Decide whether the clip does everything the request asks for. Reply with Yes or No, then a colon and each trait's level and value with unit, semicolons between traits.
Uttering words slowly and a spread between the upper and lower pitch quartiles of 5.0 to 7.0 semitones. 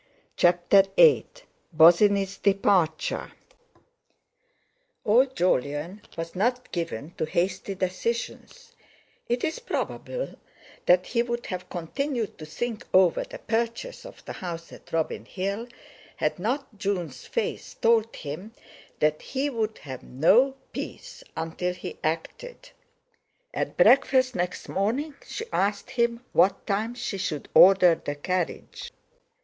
Yes: slow, 120 wpm; wide, 5.6 semitones